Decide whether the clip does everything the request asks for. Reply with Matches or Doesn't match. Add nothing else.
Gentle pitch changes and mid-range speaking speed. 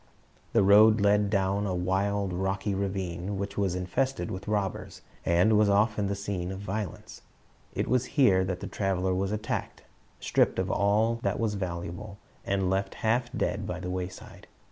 Matches